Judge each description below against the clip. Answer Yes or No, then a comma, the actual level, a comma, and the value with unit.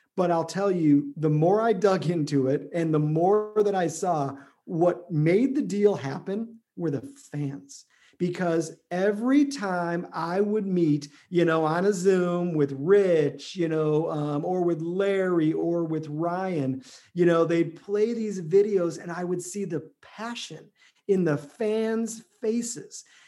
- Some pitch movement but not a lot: Yes, average, 4.1 semitones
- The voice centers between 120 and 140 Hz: No, medium, 175 Hz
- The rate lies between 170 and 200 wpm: No, average, 160 wpm